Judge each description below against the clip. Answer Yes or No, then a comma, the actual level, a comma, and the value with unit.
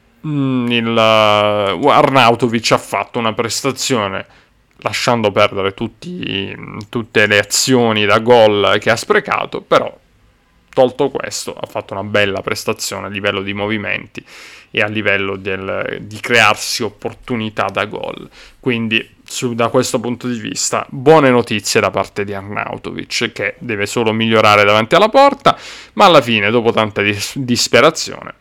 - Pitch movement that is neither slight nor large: Yes, average, 3.3 semitones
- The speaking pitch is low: Yes, low, 110 Hz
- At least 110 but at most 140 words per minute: Yes, average, 135 wpm